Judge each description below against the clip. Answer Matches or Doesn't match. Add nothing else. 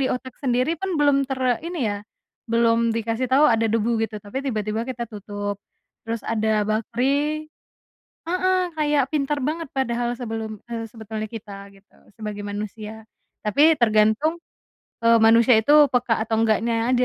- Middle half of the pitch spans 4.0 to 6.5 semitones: Doesn't match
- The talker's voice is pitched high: Matches